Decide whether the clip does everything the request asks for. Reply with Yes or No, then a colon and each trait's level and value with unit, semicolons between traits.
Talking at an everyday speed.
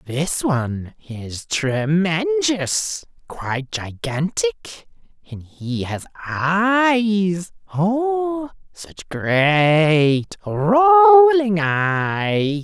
No: slow, 70 wpm